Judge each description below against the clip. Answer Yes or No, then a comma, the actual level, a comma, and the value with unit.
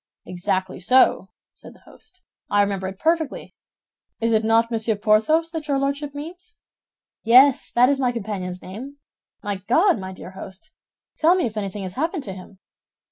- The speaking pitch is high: Yes, high, 230 Hz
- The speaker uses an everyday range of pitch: No, wide, 6.6 semitones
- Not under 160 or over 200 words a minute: Yes, average, 170 wpm